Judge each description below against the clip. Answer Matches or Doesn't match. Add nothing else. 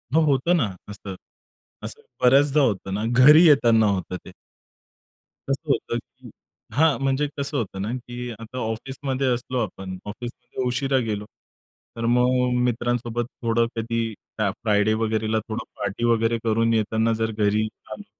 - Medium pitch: Doesn't match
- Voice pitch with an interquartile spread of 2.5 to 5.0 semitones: Matches